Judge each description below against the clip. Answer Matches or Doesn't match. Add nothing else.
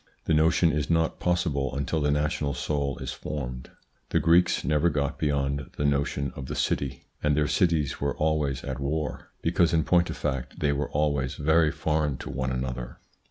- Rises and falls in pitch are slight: Matches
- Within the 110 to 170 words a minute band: Doesn't match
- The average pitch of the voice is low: Matches